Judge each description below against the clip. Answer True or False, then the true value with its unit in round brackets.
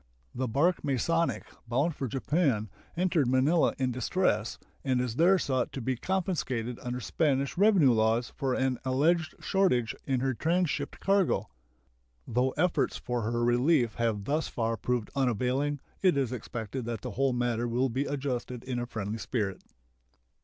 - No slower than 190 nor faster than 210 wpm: False (155 wpm)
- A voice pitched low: True (130 Hz)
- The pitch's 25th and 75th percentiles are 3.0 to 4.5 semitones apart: True (3.8 semitones)